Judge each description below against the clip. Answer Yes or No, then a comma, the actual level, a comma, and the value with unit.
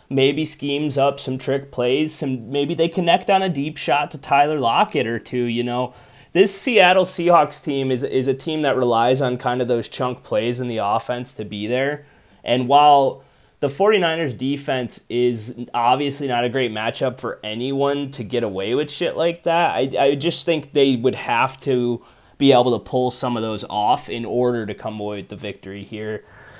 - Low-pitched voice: Yes, low, 130 Hz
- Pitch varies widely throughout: No, average, 3.2 semitones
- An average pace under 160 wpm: No, average, 200 wpm